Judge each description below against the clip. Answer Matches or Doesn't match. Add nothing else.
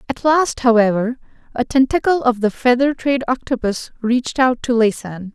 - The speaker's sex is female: Matches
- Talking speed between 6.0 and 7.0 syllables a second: Doesn't match